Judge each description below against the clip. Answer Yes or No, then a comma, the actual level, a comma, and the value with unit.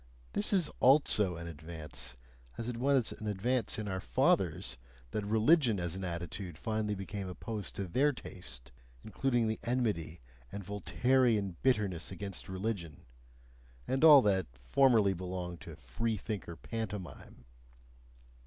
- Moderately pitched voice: No, low, 100 Hz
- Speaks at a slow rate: Yes, slow, 130 wpm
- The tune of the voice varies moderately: Yes, average, 4.8 semitones